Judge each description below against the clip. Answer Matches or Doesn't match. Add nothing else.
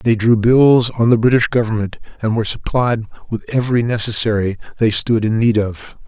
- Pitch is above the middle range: Doesn't match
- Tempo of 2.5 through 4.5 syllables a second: Doesn't match